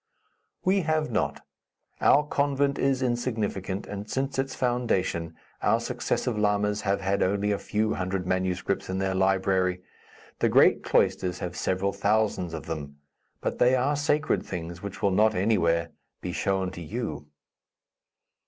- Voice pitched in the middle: No, low, 100 Hz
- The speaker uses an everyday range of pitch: Yes, average, 4.8 semitones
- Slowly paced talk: No, average, 145 wpm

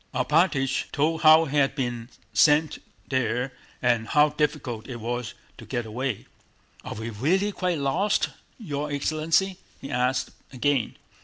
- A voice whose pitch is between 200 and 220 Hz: No, medium, 140 Hz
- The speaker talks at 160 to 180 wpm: No, average, 140 wpm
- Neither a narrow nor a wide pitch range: Yes, average, 4.2 semitones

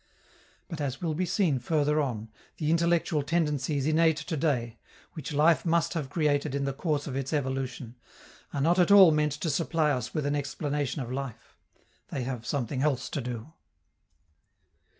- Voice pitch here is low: No, medium, 145 Hz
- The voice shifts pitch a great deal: No, average, 3.1 semitones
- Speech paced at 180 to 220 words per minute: No, average, 170 wpm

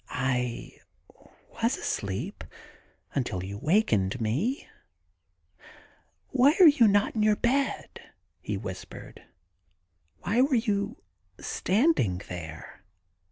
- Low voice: Yes, low, 130 Hz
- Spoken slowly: Yes, slow, 105 wpm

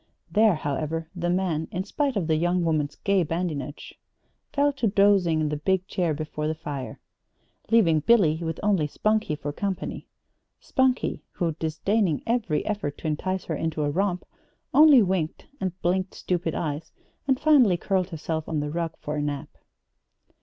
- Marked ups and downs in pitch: No, average, 4.3 semitones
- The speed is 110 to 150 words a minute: No, average, 165 wpm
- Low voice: No, medium, 170 Hz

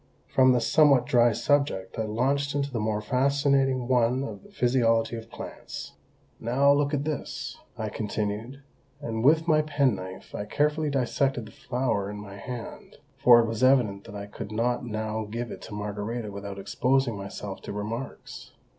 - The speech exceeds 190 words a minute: No, average, 170 wpm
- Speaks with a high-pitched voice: No, low, 120 Hz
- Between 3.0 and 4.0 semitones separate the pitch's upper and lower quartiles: No, average, 4.4 semitones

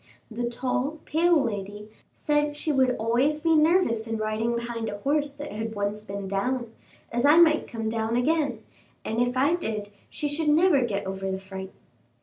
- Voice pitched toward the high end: Yes, high, 240 Hz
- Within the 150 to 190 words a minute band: Yes, average, 180 wpm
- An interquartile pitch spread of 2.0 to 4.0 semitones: No, wide, 5.5 semitones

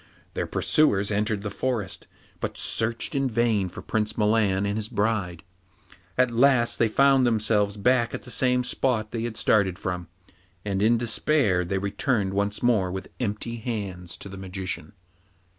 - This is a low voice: Yes, low, 110 Hz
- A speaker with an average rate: Yes, average, 160 wpm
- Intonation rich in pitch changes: No, average, 3.2 semitones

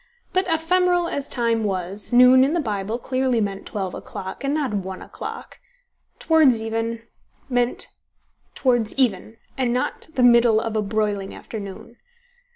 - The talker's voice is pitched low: No, high, 235 Hz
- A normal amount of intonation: Yes, average, 3.9 semitones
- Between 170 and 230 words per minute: No, average, 145 wpm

